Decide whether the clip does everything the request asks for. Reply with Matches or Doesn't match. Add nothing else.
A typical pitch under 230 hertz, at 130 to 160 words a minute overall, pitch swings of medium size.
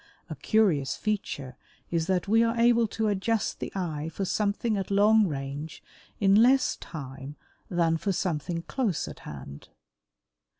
Doesn't match